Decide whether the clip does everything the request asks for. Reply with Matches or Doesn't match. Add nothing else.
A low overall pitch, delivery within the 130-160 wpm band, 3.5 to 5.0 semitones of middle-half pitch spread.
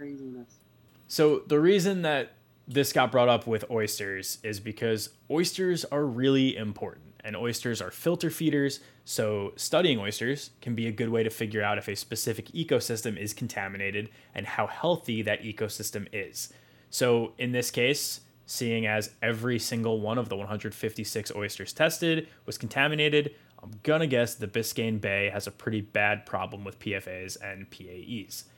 Matches